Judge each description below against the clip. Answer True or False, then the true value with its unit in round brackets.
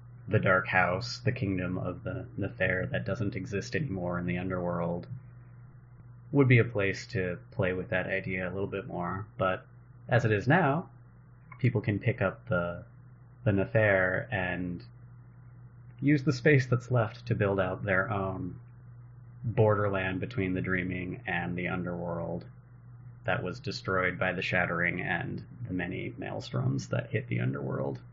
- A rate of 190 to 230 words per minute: False (150 wpm)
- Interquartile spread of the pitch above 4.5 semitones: True (4.9 semitones)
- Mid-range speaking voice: False (105 Hz)